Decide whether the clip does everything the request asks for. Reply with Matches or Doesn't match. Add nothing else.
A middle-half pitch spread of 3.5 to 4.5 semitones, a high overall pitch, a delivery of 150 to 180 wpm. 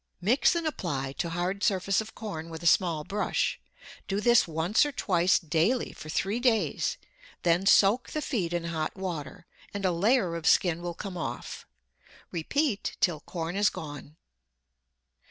Doesn't match